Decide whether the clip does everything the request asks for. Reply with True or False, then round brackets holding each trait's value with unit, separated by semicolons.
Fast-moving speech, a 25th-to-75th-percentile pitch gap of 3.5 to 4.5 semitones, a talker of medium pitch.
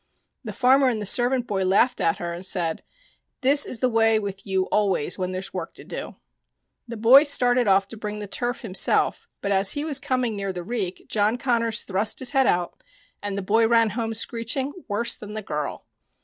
False (210 wpm; 4.0 semitones; 220 Hz)